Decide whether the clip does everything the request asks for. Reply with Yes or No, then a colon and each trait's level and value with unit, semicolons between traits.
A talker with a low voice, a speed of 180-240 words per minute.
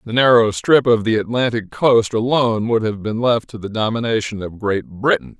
Yes: low, 110 Hz; average, 200 wpm